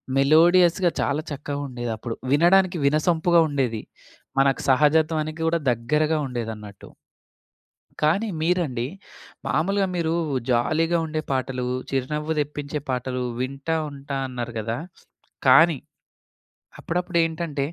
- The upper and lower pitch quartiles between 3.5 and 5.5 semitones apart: Yes, average, 4.2 semitones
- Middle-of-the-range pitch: Yes, medium, 150 Hz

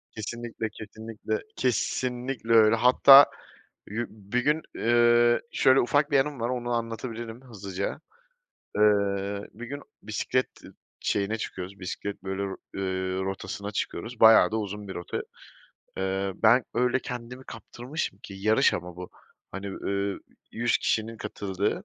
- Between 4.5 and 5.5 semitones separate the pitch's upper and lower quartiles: No, average, 3.5 semitones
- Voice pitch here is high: No, low, 110 Hz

